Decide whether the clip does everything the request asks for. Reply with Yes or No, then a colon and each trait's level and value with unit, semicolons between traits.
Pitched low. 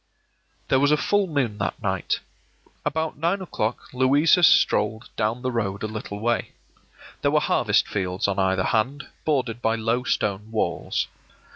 Yes: low, 115 Hz